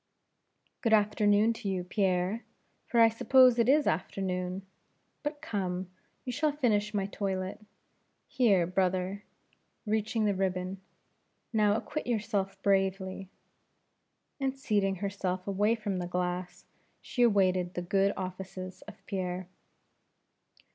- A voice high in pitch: Yes, high, 195 Hz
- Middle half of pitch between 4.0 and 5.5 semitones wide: No, average, 3.0 semitones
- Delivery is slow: Yes, slow, 125 wpm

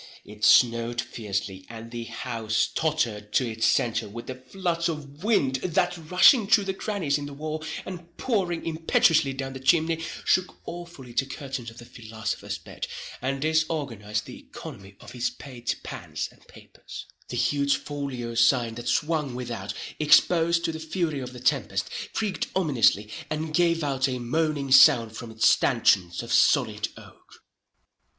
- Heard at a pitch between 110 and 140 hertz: Yes, low, 135 Hz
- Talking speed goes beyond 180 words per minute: No, average, 160 wpm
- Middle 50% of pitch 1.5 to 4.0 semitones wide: No, wide, 5.6 semitones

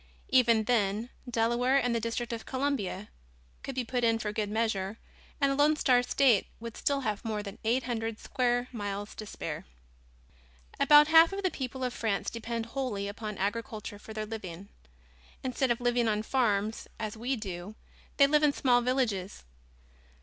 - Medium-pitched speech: No, high, 230 Hz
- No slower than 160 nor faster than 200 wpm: Yes, average, 170 wpm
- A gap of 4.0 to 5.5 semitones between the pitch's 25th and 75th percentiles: No, average, 3.3 semitones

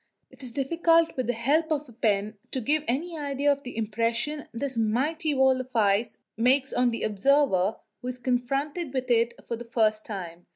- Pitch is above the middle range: Yes, very high, 250 Hz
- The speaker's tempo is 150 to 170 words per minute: No, average, 195 wpm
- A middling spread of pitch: Yes, average, 3.8 semitones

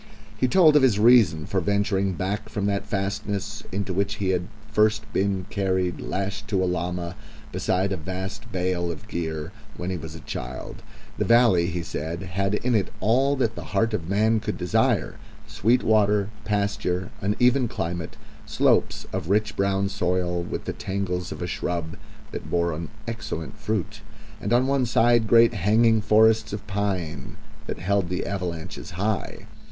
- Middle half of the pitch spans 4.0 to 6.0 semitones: No, average, 3.3 semitones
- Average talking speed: Yes, average, 170 wpm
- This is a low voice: Yes, low, 100 Hz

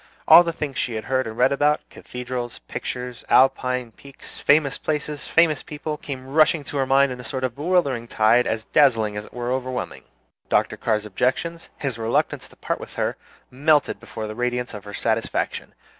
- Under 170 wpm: No, average, 190 wpm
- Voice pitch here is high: No, low, 130 Hz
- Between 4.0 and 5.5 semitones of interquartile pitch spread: No, average, 3.6 semitones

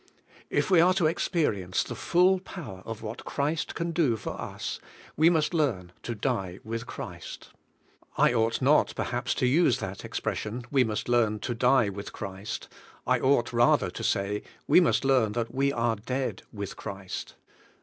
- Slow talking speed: No, average, 175 wpm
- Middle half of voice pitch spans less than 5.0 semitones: No, average, 5.3 semitones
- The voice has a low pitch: Yes, low, 120 Hz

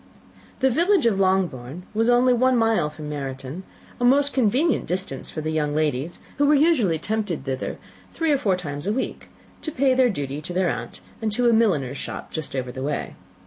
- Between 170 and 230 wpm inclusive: Yes, average, 200 wpm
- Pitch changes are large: Yes, wide, 8.8 semitones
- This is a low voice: No, high, 190 Hz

